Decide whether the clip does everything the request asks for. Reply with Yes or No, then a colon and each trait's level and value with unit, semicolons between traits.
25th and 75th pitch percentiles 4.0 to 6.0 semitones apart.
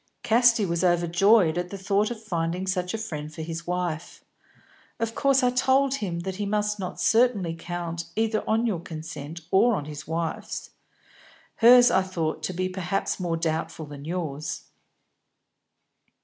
Yes: average, 4.6 semitones